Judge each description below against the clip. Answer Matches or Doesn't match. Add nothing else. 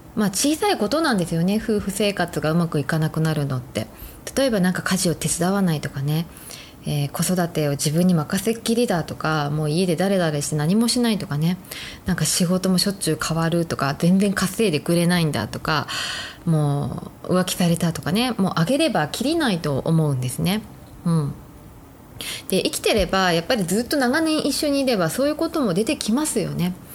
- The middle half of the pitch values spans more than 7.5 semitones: Doesn't match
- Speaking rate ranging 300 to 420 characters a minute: Matches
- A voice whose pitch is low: Doesn't match